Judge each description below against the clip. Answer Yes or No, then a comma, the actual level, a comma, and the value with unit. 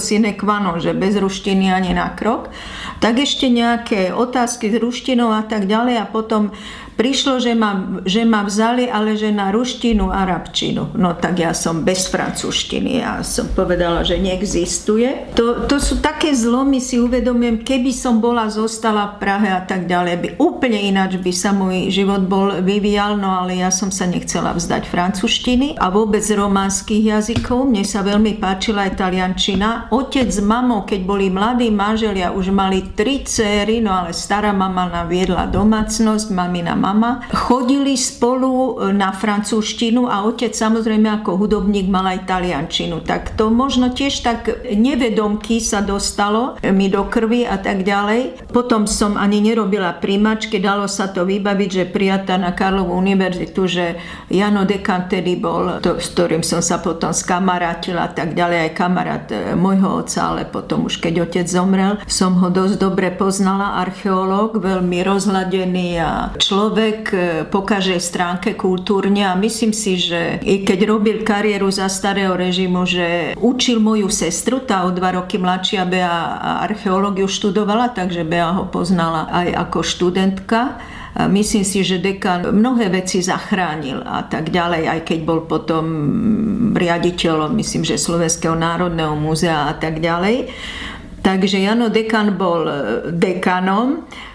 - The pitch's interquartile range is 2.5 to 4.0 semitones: Yes, average, 3.3 semitones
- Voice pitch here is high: Yes, high, 200 Hz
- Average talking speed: Yes, average, 155 wpm